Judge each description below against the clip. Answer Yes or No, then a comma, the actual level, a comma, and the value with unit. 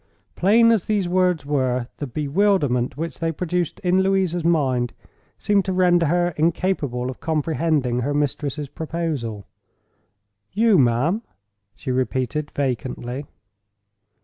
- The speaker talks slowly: Yes, slow, 120 wpm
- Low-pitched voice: No, medium, 155 Hz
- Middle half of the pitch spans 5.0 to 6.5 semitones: Yes, wide, 5.6 semitones